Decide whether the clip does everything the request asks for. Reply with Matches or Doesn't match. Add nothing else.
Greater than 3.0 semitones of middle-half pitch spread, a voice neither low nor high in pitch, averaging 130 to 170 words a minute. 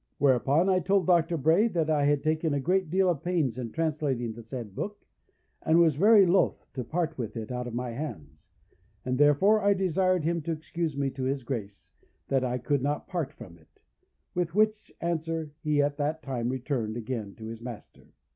Doesn't match